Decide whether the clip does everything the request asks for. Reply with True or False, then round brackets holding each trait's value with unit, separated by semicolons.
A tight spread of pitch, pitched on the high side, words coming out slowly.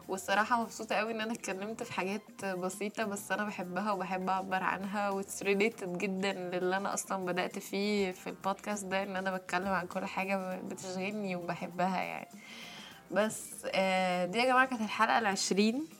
False (2.1 semitones; 195 Hz; 155 wpm)